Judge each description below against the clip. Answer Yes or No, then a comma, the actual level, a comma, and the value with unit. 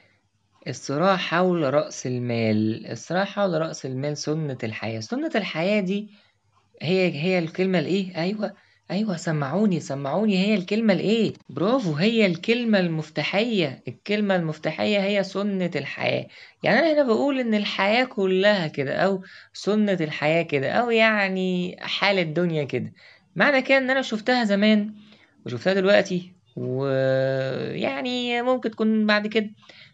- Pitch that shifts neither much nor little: No, wide, 5.7 semitones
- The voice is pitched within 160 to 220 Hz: Yes, high, 190 Hz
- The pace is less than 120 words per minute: No, average, 130 wpm